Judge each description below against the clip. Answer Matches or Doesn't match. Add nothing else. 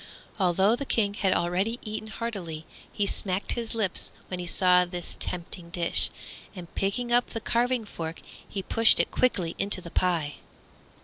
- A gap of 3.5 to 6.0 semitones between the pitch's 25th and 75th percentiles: Matches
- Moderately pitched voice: Doesn't match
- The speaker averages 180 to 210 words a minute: Doesn't match